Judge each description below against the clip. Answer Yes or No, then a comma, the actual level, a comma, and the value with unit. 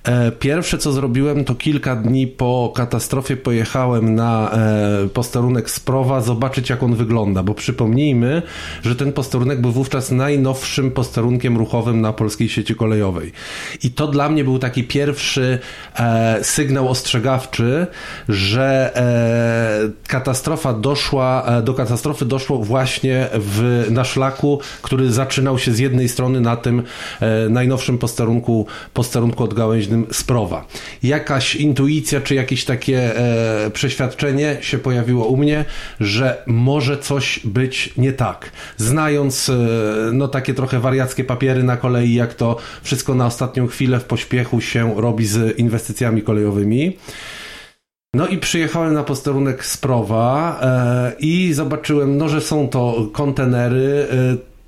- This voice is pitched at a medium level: No, low, 130 Hz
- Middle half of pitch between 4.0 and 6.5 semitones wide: No, average, 2.7 semitones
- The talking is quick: No, average, 130 wpm